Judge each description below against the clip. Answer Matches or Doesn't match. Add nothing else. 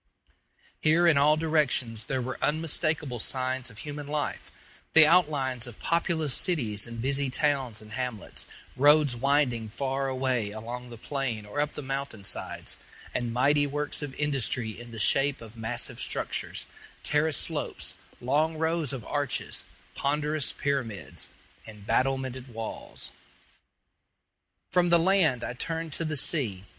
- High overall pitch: Doesn't match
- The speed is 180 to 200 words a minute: Doesn't match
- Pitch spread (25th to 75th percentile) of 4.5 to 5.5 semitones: Doesn't match